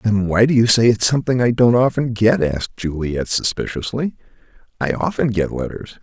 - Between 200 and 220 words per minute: No, average, 180 wpm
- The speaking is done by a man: Yes, male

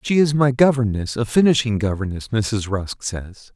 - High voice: No, low, 115 Hz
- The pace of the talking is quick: No, average, 150 wpm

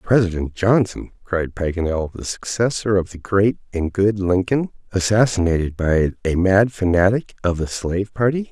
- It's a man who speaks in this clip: Yes, male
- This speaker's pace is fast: No, average, 150 wpm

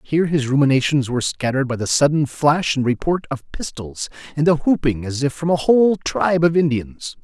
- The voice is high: No, medium, 140 Hz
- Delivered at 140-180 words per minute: No, average, 200 wpm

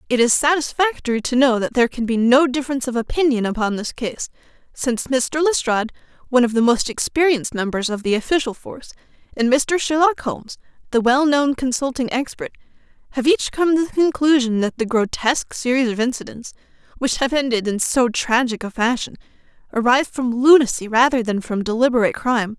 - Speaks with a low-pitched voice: No, very high, 250 Hz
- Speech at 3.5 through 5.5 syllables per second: No, 5.9 syllables/s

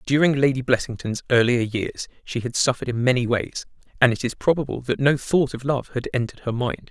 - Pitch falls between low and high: No, low, 125 Hz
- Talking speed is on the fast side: Yes, fast, 210 wpm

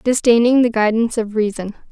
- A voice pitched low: No, high, 225 Hz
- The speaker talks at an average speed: Yes, average, 155 wpm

